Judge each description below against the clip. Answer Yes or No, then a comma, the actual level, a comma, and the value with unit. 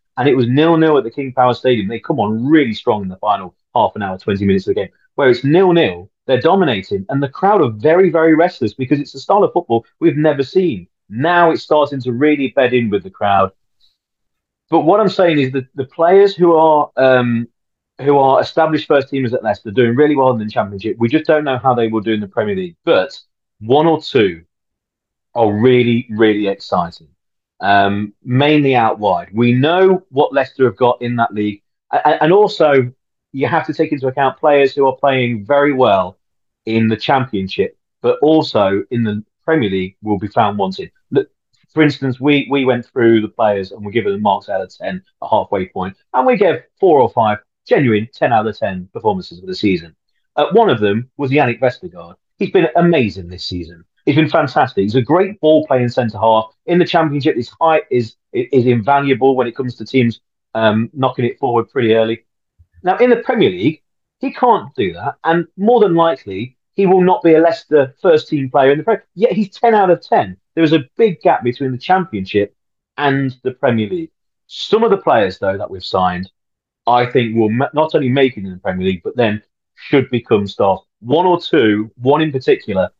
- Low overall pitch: Yes, low, 130 Hz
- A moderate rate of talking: No, fast, 210 wpm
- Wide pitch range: Yes, wide, 6.2 semitones